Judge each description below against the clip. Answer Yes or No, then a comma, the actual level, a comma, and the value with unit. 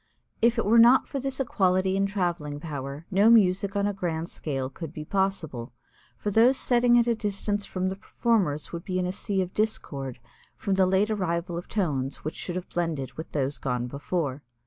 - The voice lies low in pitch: No, medium, 185 Hz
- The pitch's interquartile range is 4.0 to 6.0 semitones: Yes, average, 5.1 semitones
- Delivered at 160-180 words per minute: No, average, 200 wpm